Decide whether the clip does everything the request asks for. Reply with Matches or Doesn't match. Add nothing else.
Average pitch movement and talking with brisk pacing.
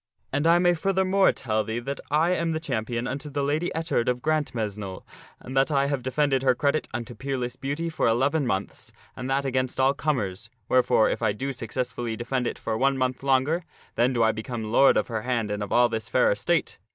Matches